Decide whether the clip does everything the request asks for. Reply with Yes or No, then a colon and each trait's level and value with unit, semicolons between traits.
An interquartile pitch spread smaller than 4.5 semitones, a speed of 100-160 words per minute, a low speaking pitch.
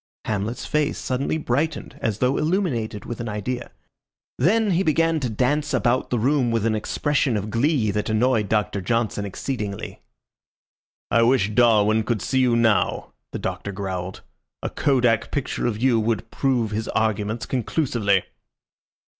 Yes: average, 3.8 semitones; average, 150 wpm; low, 115 Hz